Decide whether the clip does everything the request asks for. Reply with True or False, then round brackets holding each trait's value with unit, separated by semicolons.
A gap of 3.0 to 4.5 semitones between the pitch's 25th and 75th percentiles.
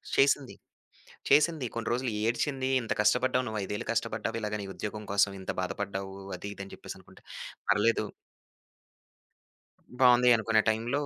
True (3.6 semitones)